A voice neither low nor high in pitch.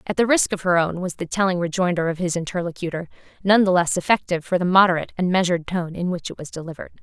Yes: medium, 180 Hz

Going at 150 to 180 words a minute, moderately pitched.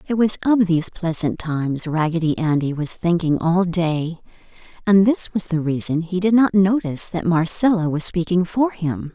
Yes: average, 175 wpm; medium, 175 Hz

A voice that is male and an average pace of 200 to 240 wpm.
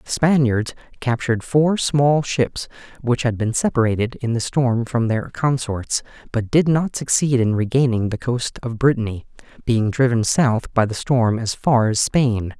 No: male; average, 170 wpm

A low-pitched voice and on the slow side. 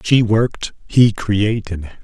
Yes: low, 105 Hz; slow, 120 wpm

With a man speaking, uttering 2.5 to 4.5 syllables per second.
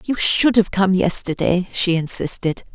No: female; 4.3 syllables/s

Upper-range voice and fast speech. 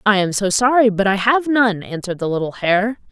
Yes: high, 210 Hz; fast, 230 wpm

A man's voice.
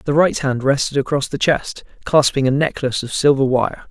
Yes: male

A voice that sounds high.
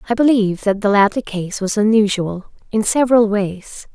Yes: high, 210 Hz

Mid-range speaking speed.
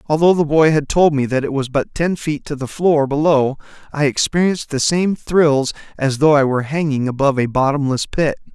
No: fast, 210 wpm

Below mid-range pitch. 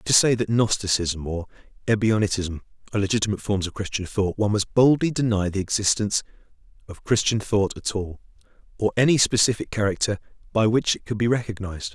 Yes: low, 105 Hz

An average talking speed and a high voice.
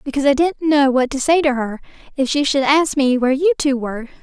No: fast, 255 wpm; very high, 275 Hz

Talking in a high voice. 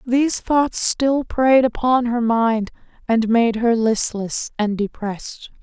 Yes: high, 235 Hz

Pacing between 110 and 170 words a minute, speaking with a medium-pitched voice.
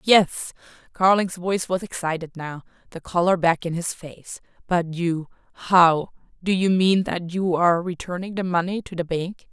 Yes: average, 160 wpm; medium, 175 Hz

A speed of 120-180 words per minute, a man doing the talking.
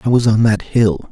No: fast, 270 wpm; male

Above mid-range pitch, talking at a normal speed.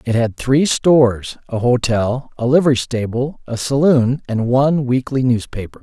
No: low, 125 Hz; average, 155 wpm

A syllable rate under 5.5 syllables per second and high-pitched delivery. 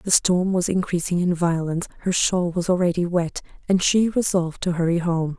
No: 5.3 syllables/s; medium, 175 Hz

